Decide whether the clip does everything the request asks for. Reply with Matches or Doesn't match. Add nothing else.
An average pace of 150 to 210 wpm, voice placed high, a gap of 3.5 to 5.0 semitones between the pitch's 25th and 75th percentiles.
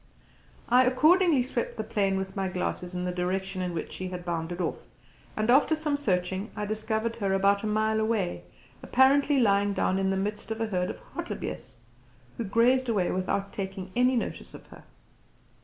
Matches